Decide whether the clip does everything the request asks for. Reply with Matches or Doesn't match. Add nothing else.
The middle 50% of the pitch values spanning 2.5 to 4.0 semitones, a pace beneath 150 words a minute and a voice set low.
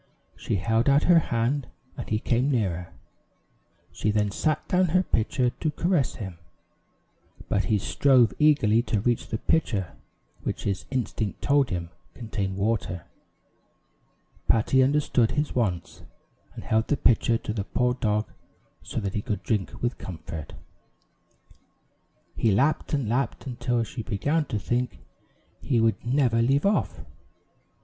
Doesn't match